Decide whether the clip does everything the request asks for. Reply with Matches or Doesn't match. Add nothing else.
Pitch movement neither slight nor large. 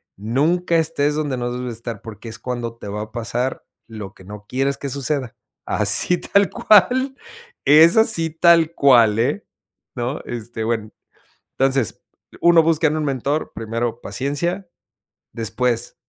Doesn't match